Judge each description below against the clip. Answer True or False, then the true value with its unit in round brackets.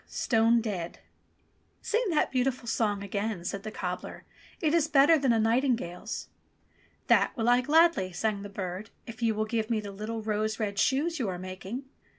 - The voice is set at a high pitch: True (220 Hz)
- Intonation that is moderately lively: True (4.0 semitones)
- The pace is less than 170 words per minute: False (180 wpm)